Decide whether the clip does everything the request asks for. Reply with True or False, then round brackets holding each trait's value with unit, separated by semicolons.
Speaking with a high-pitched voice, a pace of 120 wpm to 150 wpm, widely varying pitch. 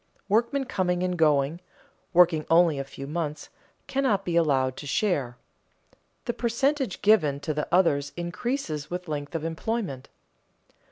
False (170 Hz; 135 wpm; 5.8 semitones)